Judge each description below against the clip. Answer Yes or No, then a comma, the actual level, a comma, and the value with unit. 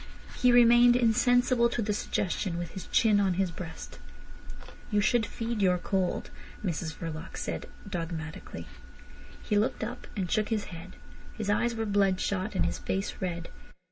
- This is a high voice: Yes, high, 205 Hz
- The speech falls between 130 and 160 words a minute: Yes, average, 155 wpm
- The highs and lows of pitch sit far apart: No, average, 4.1 semitones